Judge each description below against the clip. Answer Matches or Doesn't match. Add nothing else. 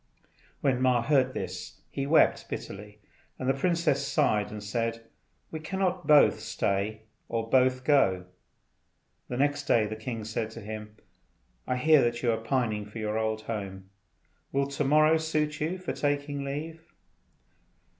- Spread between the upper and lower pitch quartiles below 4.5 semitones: Doesn't match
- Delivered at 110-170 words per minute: Matches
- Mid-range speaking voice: Doesn't match